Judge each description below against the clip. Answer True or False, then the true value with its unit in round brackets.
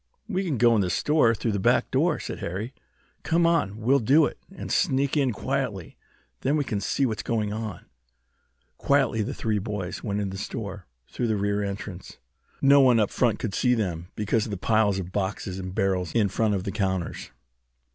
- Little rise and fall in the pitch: False (4.3 semitones)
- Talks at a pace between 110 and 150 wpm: False (200 wpm)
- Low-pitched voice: True (110 Hz)